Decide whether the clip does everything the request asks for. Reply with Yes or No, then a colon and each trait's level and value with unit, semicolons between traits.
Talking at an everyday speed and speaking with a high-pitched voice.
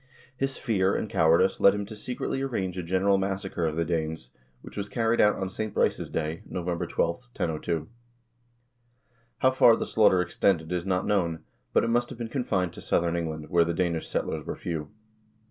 No: average, 190 wpm; very low, 95 Hz